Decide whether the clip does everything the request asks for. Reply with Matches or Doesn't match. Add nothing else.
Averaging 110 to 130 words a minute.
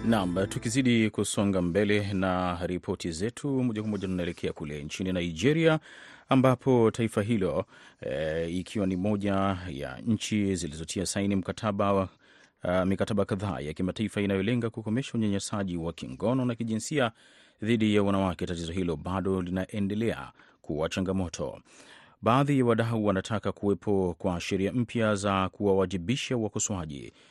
Matches